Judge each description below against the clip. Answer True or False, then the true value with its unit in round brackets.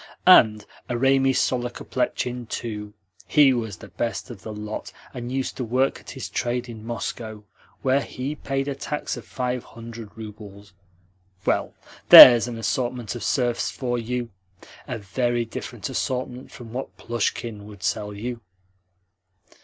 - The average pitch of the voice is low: True (120 Hz)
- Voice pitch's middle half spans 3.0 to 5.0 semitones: False (2.6 semitones)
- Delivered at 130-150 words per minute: True (145 wpm)